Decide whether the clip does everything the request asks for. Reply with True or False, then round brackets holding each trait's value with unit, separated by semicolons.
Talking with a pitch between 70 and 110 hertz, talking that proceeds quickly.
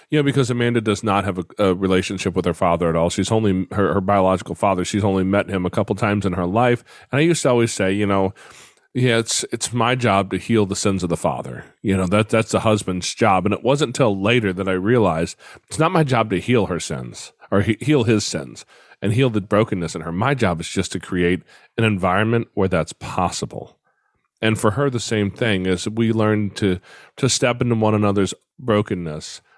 True (105 Hz; 230 wpm)